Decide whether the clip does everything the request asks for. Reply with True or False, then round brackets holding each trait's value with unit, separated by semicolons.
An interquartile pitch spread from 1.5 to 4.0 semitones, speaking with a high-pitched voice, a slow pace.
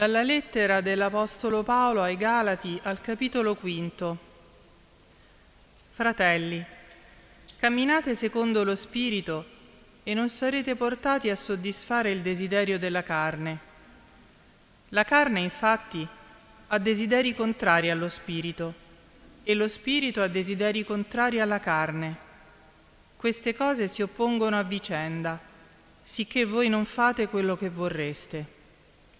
False (5.3 semitones; 205 Hz; 110 wpm)